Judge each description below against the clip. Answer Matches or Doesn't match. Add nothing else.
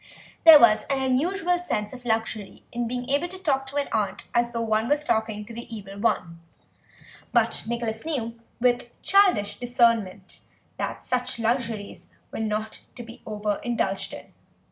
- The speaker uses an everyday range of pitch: Matches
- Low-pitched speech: Doesn't match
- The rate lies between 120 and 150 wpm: Doesn't match